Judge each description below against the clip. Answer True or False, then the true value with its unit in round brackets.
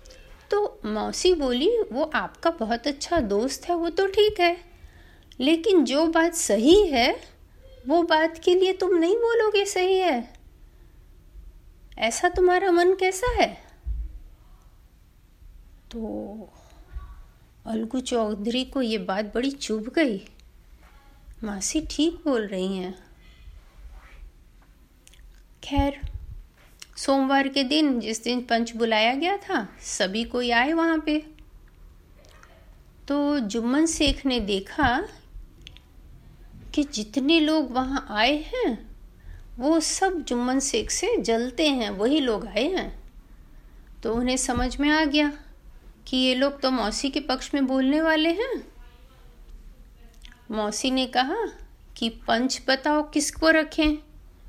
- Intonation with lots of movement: True (7.3 semitones)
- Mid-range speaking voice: False (260 Hz)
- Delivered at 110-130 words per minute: True (120 wpm)